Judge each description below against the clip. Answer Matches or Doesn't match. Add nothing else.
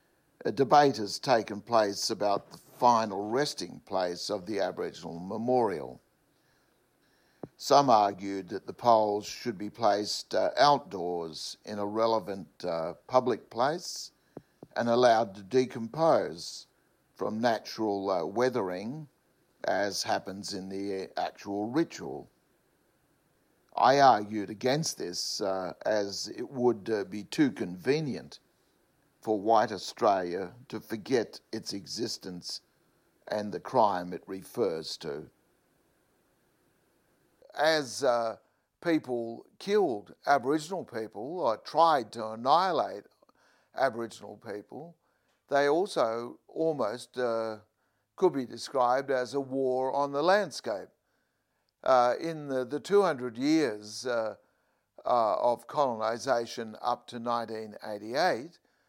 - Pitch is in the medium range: Doesn't match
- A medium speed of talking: Doesn't match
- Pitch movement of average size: Matches